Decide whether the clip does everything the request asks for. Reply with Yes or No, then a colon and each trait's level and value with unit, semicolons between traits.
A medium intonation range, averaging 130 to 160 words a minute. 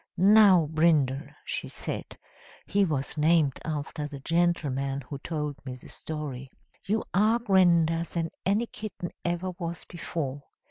Yes: average, 4.2 semitones; slow, 135 wpm